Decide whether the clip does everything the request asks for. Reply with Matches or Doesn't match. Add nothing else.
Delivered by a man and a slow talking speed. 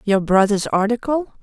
Doesn't match